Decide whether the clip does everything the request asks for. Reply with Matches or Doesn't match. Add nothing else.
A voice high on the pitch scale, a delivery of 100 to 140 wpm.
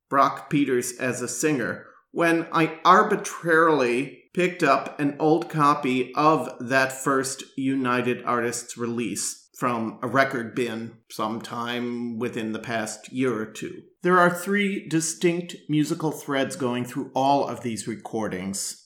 Doesn't match